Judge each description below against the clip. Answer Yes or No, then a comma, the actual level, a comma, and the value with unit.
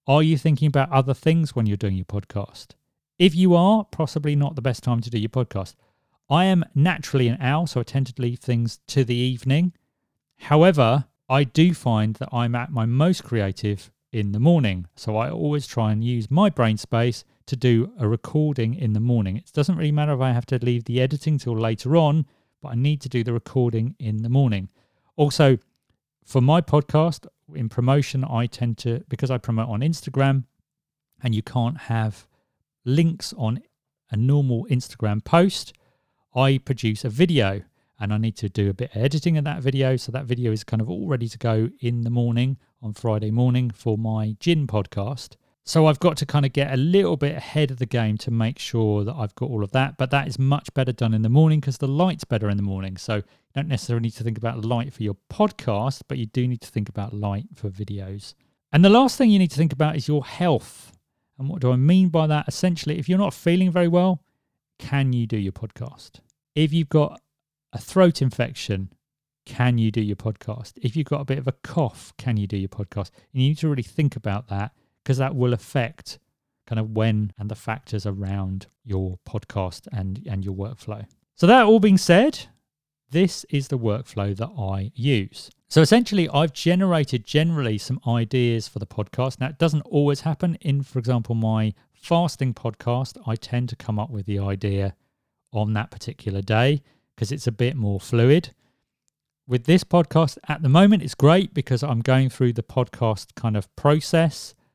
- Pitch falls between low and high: No, low, 125 Hz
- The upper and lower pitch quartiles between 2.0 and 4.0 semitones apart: No, average, 4.9 semitones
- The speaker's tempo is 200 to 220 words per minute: Yes, fast, 205 wpm